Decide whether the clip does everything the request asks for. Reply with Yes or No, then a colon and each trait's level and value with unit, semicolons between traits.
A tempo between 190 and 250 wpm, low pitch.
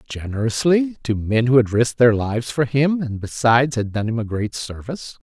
Yes: fast, 205 wpm; low, 120 Hz